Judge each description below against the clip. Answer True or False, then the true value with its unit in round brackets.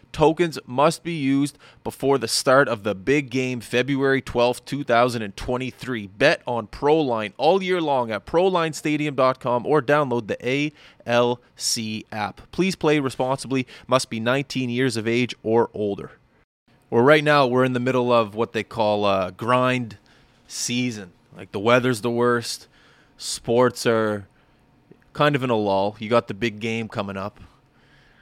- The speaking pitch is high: False (125 Hz)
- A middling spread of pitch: True (3.4 semitones)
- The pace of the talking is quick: False (155 wpm)